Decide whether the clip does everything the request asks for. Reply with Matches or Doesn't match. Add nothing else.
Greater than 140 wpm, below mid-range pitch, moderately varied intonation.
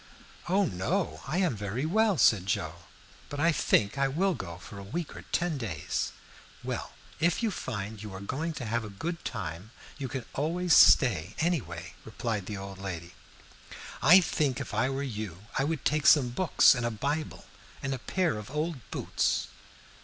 Doesn't match